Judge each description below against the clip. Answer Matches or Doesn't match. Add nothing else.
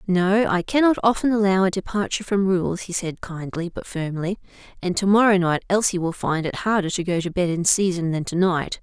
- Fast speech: Matches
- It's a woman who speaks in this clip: Matches